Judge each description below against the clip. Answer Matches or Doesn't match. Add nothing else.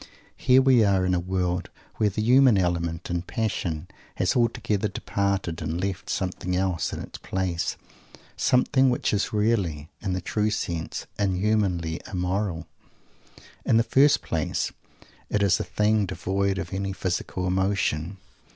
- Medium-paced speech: Matches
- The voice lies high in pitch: Doesn't match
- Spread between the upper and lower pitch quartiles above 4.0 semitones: Doesn't match